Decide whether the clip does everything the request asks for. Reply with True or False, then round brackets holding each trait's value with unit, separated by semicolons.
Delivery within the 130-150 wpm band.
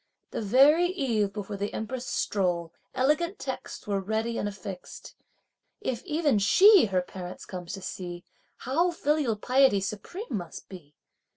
True (145 wpm)